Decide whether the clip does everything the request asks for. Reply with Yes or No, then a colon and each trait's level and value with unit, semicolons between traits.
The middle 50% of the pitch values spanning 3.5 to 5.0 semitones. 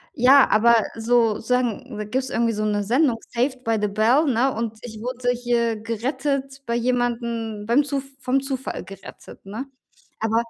No: narrow, 2.5 semitones